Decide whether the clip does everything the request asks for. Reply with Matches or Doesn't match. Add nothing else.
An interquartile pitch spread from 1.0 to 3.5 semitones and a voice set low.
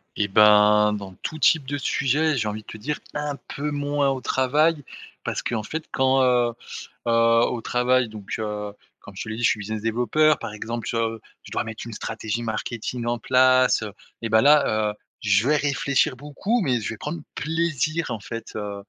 Doesn't match